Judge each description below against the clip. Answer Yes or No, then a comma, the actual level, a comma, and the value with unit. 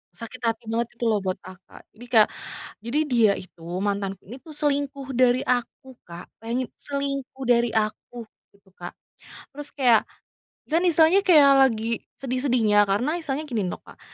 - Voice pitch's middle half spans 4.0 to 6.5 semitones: Yes, average, 4.3 semitones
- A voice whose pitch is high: Yes, high, 245 Hz